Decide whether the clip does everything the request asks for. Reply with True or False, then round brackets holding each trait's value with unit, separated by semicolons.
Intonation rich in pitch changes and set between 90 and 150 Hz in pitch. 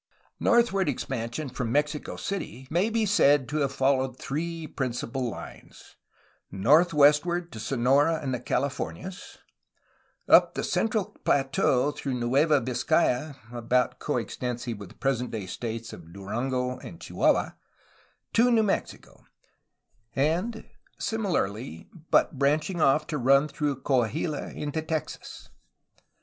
False (4.2 semitones; 140 Hz)